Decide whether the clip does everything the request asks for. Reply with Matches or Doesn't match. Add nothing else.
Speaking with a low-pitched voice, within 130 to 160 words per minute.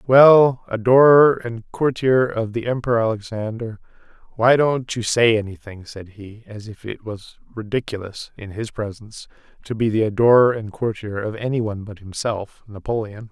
Matches